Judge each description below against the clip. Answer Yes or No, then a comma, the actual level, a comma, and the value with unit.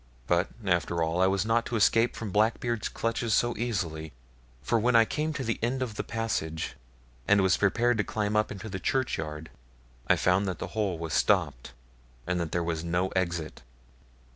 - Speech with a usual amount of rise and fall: Yes, average, 5.0 semitones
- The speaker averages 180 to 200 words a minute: Yes, average, 190 wpm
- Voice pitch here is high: No, low, 100 Hz